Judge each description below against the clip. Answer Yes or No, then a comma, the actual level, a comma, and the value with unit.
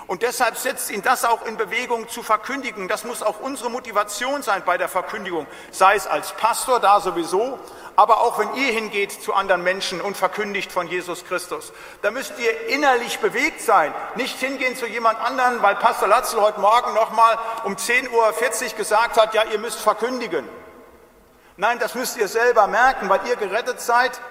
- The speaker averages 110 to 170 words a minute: No, average, 185 wpm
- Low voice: No, high, 225 Hz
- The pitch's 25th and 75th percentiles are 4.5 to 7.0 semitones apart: No, average, 3.6 semitones